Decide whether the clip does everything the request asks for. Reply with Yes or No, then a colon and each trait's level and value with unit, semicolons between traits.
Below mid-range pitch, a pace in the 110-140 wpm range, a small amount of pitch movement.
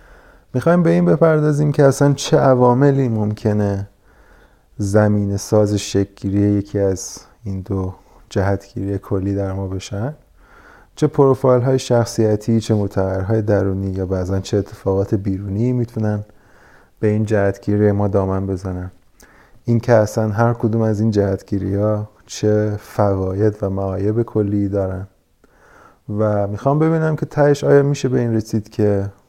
No: low, 105 Hz; average, 135 wpm; average, 3.1 semitones